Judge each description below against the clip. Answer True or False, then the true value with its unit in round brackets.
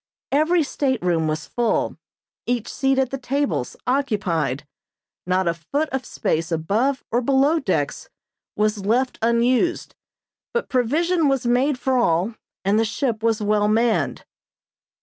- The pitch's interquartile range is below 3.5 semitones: False (4.9 semitones)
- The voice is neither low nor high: False (240 Hz)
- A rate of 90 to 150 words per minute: True (135 wpm)